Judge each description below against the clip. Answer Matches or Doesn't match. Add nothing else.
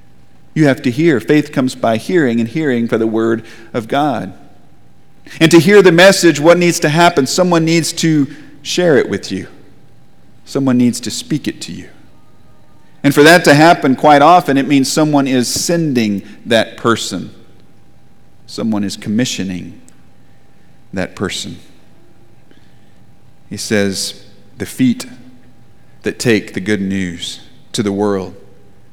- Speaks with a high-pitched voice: Doesn't match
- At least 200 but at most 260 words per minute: Doesn't match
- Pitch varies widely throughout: Matches